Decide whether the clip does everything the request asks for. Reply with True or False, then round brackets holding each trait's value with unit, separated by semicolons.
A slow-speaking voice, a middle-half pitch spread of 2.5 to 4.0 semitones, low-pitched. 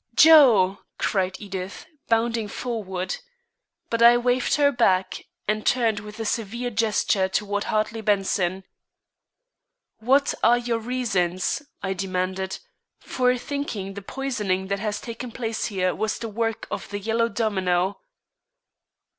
False (130 wpm; 3.7 semitones; 215 Hz)